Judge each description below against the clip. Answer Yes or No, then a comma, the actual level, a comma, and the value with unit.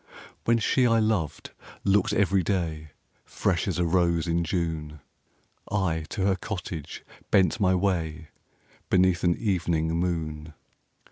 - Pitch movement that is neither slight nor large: Yes, average, 3.1 semitones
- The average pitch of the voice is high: No, very low, 90 Hz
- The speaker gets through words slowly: Yes, slow, 130 wpm